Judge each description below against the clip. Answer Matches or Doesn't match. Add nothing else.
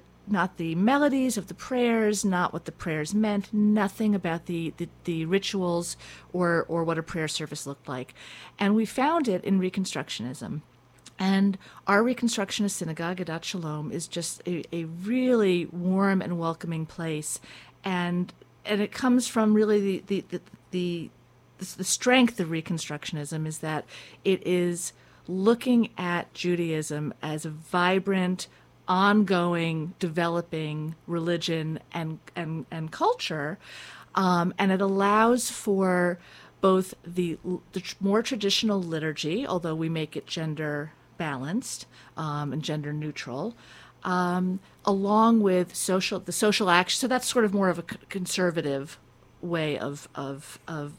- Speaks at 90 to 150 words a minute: Matches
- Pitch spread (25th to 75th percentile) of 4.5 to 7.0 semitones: Doesn't match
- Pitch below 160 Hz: Doesn't match